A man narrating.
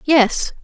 No: female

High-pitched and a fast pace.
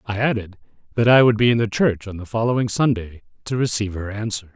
No: low, 110 Hz; fast, 225 wpm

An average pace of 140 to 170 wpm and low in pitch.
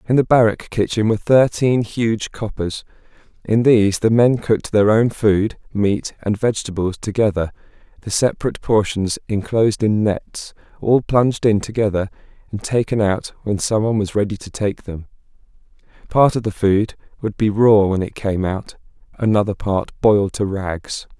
Yes: average, 160 wpm; low, 105 Hz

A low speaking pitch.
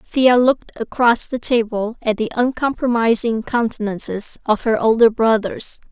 No: high, 230 Hz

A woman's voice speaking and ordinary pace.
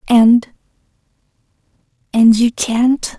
No: female; slow, 75 wpm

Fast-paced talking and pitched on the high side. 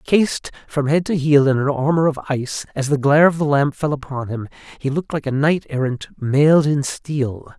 No: fast, 220 wpm; medium, 145 Hz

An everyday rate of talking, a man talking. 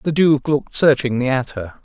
Yes: average, 195 wpm; male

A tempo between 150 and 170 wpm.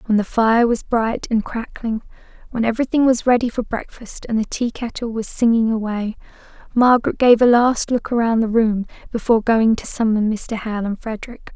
No: average, 180 wpm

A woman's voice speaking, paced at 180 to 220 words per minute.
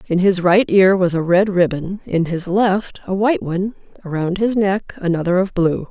Yes: female; fast, 205 wpm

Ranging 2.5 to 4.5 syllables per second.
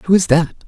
No: 5.6 syllables/s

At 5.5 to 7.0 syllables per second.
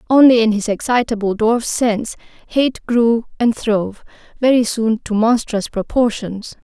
No: 4.4 syllables/s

